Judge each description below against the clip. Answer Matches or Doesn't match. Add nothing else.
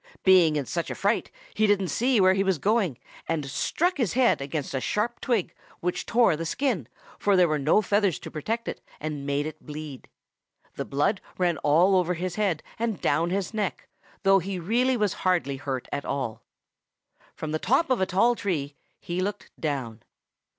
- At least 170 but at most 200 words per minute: Matches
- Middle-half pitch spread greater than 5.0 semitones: Matches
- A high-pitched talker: Doesn't match